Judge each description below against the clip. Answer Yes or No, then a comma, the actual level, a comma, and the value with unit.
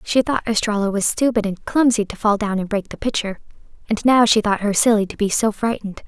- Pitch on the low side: No, high, 215 Hz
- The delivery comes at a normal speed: No, fast, 235 wpm